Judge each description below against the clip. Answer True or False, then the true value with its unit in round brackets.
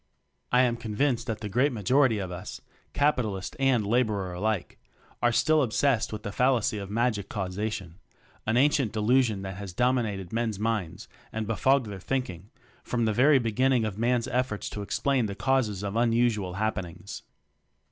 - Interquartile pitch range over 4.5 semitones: False (3.7 semitones)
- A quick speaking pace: False (170 wpm)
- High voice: False (110 Hz)